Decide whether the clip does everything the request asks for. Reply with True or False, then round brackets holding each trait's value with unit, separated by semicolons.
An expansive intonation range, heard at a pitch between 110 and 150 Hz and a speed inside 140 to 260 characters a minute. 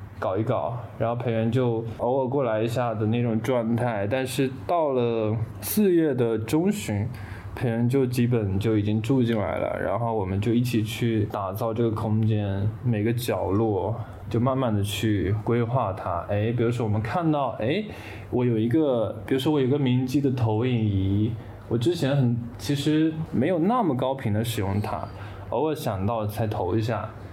False (2.6 semitones; 115 Hz; 255 characters per minute)